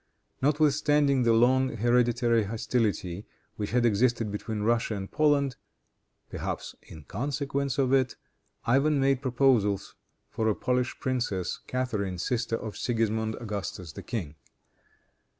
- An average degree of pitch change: Yes, average, 3.8 semitones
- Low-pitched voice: Yes, low, 120 Hz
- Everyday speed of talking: No, slow, 120 wpm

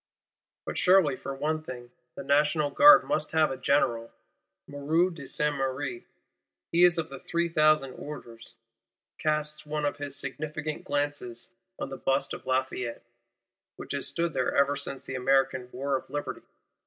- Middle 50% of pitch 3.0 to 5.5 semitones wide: No, narrow, 2.6 semitones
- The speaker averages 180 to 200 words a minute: No, average, 155 wpm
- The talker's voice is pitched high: No, medium, 145 Hz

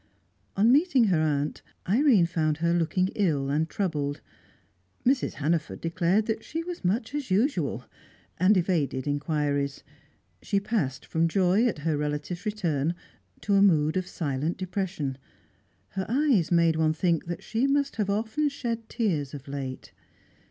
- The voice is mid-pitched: Yes, medium, 175 Hz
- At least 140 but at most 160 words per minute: Yes, average, 150 wpm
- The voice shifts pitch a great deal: Yes, wide, 6.2 semitones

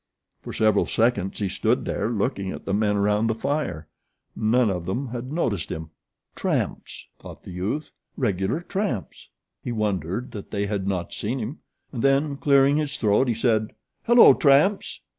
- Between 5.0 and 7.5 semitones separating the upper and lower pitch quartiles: Yes, wide, 5.4 semitones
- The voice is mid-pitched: No, low, 110 Hz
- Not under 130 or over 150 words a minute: No, average, 165 wpm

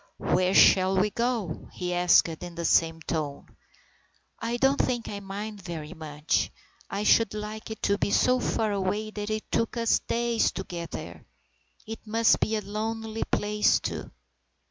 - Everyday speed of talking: Yes, average, 170 wpm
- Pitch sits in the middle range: No, high, 210 Hz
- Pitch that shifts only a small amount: No, average, 3.8 semitones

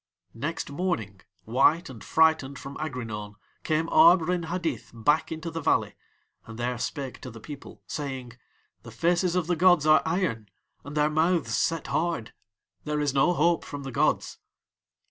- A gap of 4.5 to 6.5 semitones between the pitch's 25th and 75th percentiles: Yes, average, 4.9 semitones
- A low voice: No, medium, 150 Hz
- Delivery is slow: No, average, 165 wpm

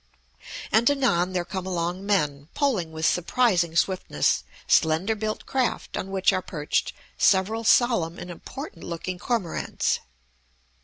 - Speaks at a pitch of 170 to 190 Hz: Yes, medium, 185 Hz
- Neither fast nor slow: No, slow, 125 wpm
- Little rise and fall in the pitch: No, average, 4.6 semitones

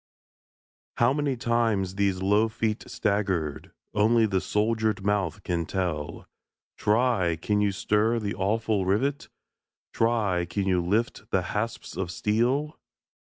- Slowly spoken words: Yes, slow, 125 wpm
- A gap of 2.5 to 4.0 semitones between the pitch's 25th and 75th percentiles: Yes, average, 3.3 semitones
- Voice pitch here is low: Yes, low, 105 Hz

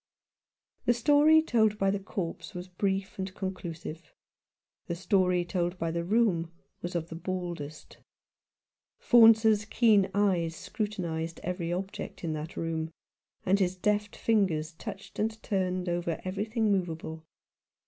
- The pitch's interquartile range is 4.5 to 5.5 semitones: No, average, 3.6 semitones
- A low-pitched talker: No, medium, 185 Hz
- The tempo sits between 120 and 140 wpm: Yes, slow, 135 wpm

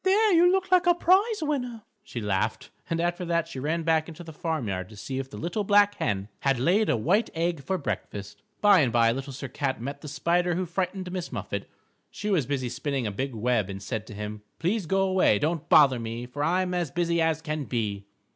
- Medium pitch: Yes, medium, 160 Hz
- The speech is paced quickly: Yes, fast, 230 wpm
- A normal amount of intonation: No, wide, 7.1 semitones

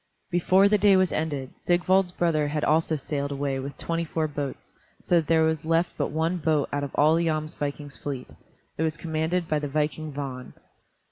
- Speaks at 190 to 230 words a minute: Yes, average, 195 wpm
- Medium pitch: Yes, medium, 155 Hz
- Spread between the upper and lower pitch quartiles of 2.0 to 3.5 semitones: Yes, narrow, 2.5 semitones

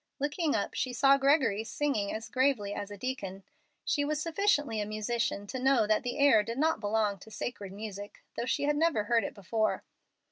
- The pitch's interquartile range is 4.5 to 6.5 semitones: Yes, average, 5.2 semitones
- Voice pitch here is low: No, high, 230 Hz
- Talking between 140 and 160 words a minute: No, average, 200 wpm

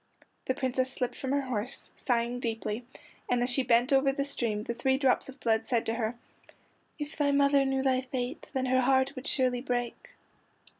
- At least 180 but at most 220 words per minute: Yes, average, 195 wpm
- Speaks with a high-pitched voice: Yes, very high, 255 Hz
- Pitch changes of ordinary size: No, narrow, 1.9 semitones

